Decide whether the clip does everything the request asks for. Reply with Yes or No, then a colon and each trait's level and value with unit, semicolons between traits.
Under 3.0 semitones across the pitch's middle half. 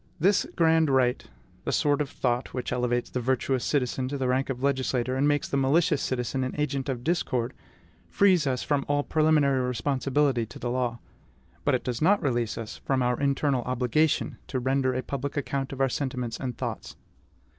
Yes: narrow, 2.4 semitones